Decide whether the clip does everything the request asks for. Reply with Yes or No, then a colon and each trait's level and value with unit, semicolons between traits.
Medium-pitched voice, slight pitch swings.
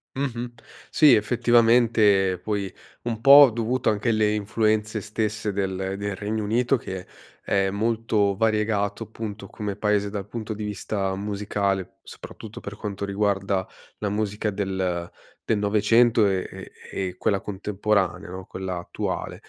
No: low, 105 Hz; narrow, 2.0 semitones